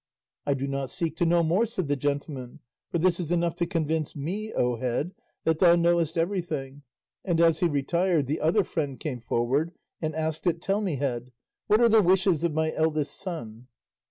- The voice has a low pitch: No, medium, 160 Hz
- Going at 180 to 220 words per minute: Yes, average, 195 wpm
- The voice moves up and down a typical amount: Yes, average, 3.7 semitones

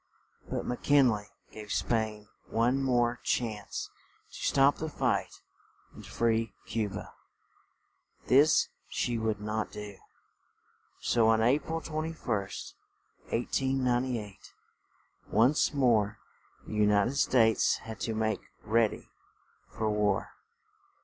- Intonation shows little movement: No, average, 3.3 semitones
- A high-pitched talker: No, low, 115 Hz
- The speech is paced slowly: Yes, slow, 120 wpm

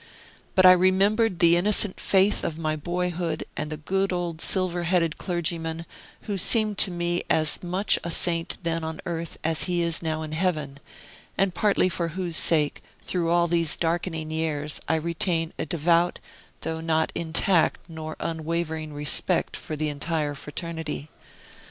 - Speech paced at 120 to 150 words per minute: No, average, 160 wpm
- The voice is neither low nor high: Yes, medium, 165 Hz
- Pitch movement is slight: Yes, narrow, 2.0 semitones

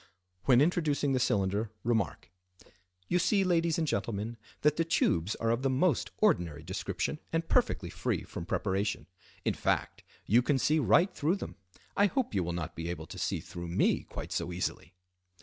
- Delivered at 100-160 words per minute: No, average, 175 wpm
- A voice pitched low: Yes, low, 115 Hz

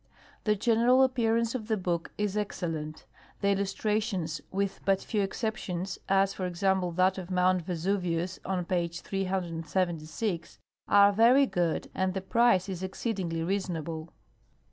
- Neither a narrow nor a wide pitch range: Yes, average, 3.1 semitones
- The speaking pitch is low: No, high, 190 Hz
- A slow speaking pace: No, average, 145 wpm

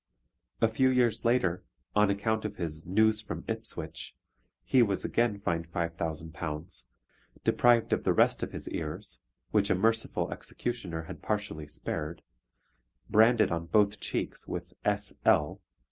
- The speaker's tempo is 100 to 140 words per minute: Yes, slow, 135 wpm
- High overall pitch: No, low, 100 Hz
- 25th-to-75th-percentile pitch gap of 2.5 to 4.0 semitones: No, average, 4.9 semitones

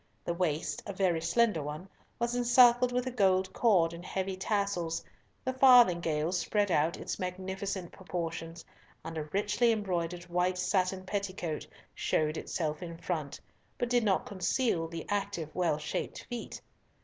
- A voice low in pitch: No, medium, 185 Hz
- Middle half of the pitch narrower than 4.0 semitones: Yes, average, 3.6 semitones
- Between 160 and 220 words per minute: No, average, 150 wpm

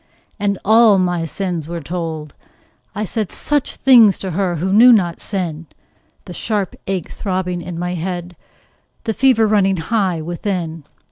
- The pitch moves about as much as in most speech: Yes, average, 3.2 semitones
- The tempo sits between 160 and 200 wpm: No, average, 150 wpm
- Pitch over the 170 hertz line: Yes, medium, 185 Hz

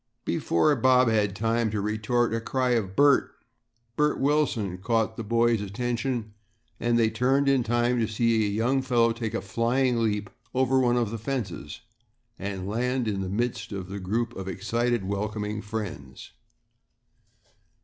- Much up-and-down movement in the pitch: No, average, 2.9 semitones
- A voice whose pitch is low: Yes, low, 115 Hz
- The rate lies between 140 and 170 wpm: Yes, average, 160 wpm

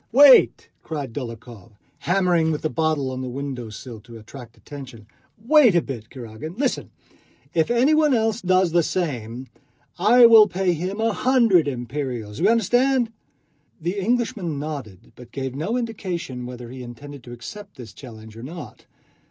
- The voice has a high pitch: No, medium, 155 Hz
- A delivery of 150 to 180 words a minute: Yes, average, 160 wpm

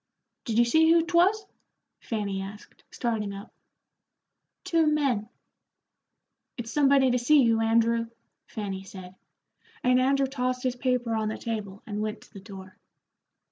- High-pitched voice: Yes, high, 235 Hz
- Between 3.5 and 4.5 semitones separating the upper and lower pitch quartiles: Yes, average, 4.2 semitones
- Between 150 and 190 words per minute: No, average, 140 wpm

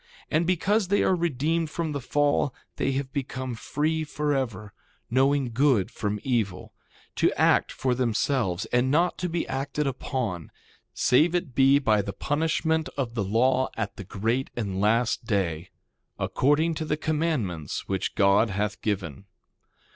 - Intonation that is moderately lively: No, wide, 6.0 semitones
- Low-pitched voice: Yes, low, 130 Hz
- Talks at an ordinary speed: Yes, average, 155 wpm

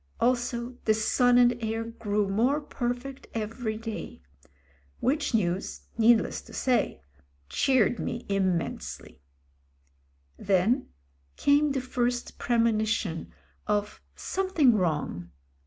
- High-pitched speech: Yes, high, 230 Hz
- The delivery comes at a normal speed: No, slow, 100 wpm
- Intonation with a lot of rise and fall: No, average, 3.0 semitones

